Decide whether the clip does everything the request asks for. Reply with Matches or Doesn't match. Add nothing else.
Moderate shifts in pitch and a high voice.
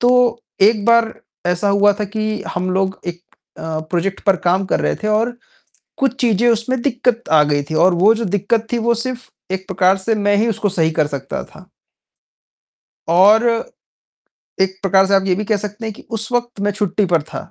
Matches